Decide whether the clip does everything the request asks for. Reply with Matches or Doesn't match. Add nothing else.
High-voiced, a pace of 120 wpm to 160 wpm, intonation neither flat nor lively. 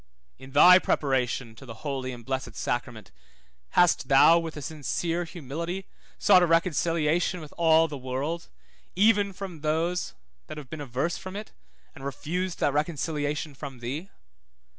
Doesn't match